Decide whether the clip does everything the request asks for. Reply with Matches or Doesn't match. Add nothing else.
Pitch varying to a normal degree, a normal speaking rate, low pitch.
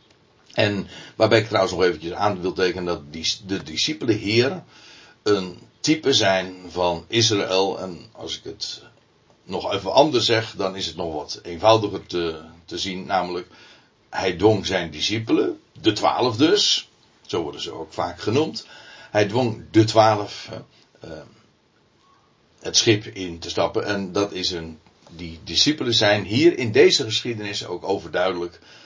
Matches